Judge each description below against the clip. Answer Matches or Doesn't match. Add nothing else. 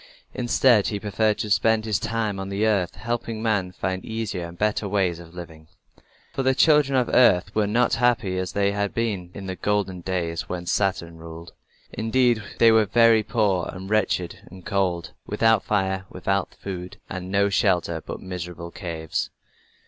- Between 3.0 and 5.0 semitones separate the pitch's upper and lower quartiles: Matches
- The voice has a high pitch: Doesn't match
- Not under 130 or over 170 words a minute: Doesn't match